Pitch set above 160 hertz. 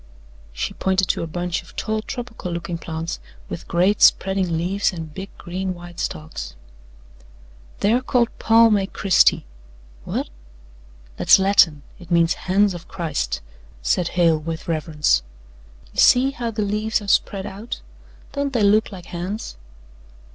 Yes: medium, 185 Hz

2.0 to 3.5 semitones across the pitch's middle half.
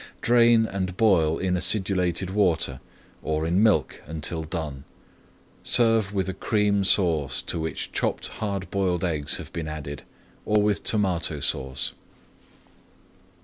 No: average, 4.4 semitones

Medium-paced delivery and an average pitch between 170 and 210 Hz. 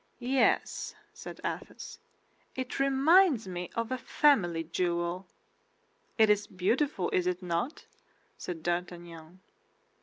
No: slow, 110 wpm; medium, 185 Hz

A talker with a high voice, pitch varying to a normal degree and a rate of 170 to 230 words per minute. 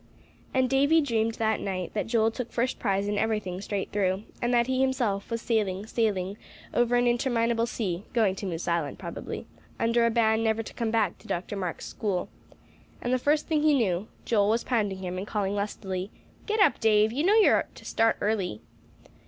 Yes: high, 220 Hz; average, 3.3 semitones; average, 200 wpm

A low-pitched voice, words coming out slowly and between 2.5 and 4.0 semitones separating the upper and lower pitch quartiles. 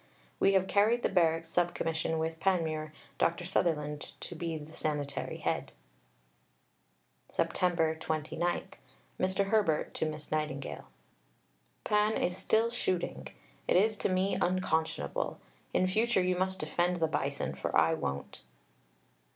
No: medium, 175 Hz; slow, 130 wpm; average, 3.1 semitones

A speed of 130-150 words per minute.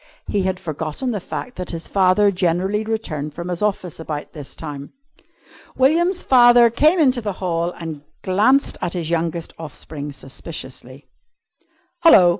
Yes: average, 145 wpm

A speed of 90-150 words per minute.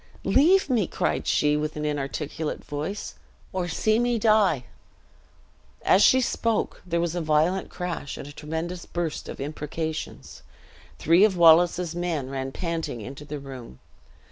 Yes: average, 145 wpm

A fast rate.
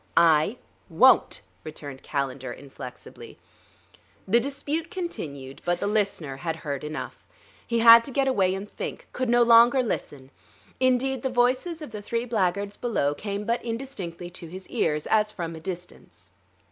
No: average, 160 wpm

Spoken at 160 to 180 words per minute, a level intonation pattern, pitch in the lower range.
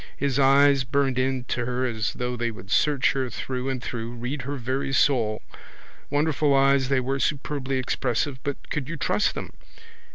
Yes: average, 170 wpm; narrow, 2.0 semitones; low, 130 Hz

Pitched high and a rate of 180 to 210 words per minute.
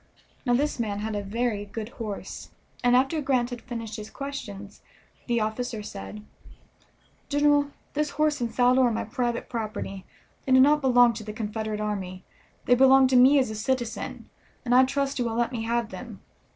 Yes: high, 240 Hz; average, 185 wpm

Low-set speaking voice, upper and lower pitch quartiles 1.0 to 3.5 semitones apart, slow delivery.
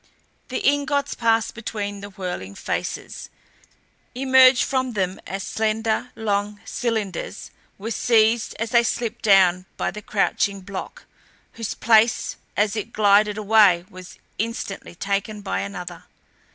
No: high, 215 Hz; narrow, 2.6 semitones; slow, 125 wpm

